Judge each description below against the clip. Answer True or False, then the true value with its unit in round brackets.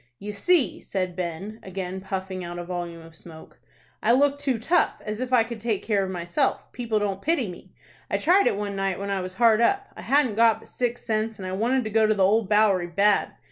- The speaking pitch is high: True (210 Hz)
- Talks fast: True (235 wpm)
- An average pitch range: True (3.8 semitones)